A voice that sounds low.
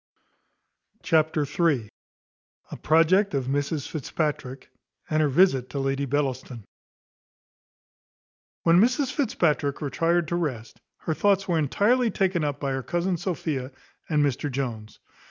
No: medium, 150 Hz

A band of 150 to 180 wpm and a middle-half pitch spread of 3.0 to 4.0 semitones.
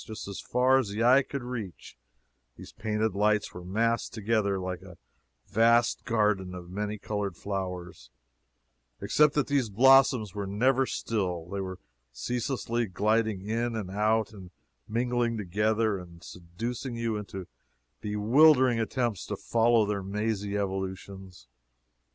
No: slow, 135 wpm; average, 3.3 semitones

